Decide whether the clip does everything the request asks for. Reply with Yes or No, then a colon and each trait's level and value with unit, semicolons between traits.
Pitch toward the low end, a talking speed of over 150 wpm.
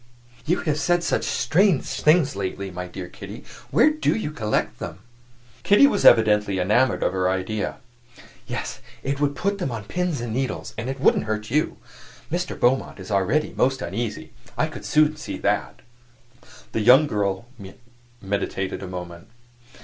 Yes: low, 120 Hz; average, 165 wpm